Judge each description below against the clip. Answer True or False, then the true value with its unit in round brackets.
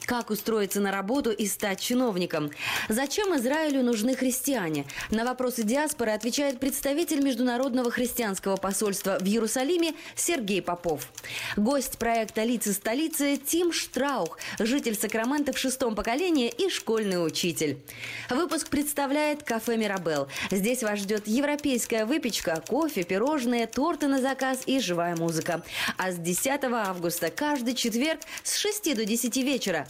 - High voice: True (240 Hz)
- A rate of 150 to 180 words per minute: False (130 wpm)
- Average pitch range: False (5.7 semitones)